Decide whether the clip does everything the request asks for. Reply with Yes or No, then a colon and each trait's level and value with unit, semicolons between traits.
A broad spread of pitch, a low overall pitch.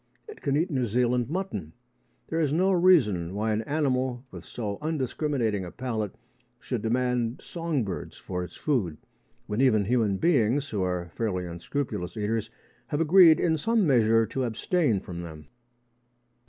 Yes: wide, 6.3 semitones; low, 120 Hz